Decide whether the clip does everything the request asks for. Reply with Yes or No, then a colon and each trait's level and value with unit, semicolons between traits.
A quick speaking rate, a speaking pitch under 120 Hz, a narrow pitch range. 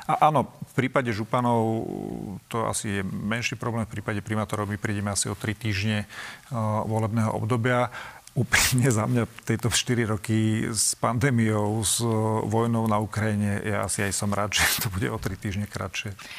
Yes: fast, 170 wpm; low, 110 Hz; narrow, 2.0 semitones